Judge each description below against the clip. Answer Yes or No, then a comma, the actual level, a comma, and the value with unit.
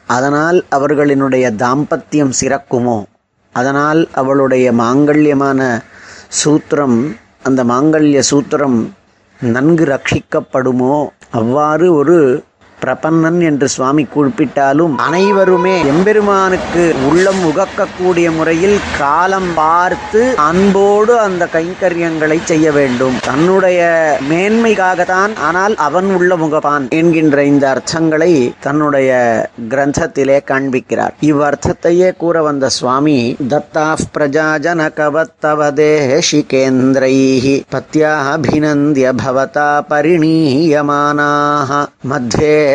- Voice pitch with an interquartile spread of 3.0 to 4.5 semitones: Yes, average, 3.6 semitones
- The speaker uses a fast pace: No, average, 80 wpm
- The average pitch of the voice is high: No, medium, 150 Hz